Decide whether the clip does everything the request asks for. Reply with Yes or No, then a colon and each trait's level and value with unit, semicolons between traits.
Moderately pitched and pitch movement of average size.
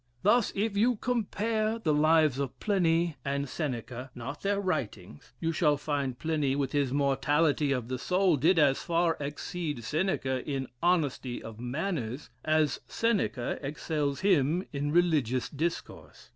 Yes: medium, 150 Hz; average, 4.5 semitones